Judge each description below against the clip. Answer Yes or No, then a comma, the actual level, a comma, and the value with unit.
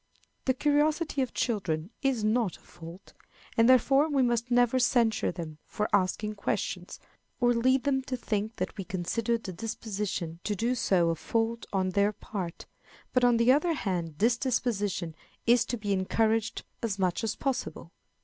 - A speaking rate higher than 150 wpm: Yes, average, 170 wpm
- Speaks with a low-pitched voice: No, high, 225 Hz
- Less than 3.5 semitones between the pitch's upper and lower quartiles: No, average, 4.3 semitones